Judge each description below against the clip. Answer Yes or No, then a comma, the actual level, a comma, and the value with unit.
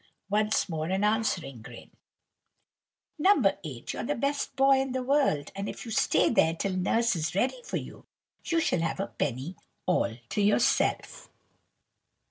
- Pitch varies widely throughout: Yes, wide, 7.8 semitones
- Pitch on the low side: No, high, 205 Hz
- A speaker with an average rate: Yes, average, 160 wpm